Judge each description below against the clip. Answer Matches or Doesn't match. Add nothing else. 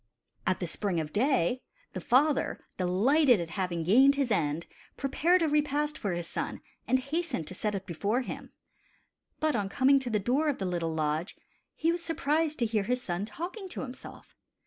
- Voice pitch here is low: Doesn't match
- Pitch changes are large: Matches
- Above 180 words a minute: Matches